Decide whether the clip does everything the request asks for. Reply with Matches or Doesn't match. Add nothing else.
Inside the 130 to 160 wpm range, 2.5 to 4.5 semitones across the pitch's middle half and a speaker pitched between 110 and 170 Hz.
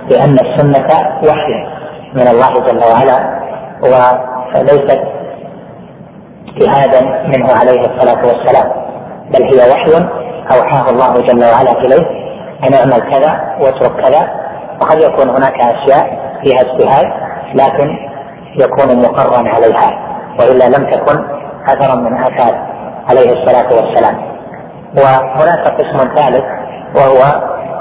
Doesn't match